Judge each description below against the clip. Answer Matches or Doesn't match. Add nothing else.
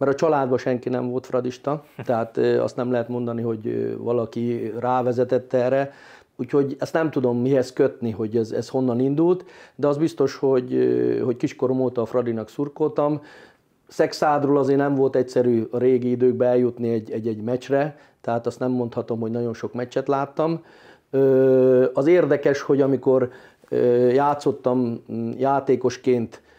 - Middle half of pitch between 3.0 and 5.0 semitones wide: Doesn't match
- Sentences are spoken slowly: Doesn't match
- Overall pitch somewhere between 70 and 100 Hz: Doesn't match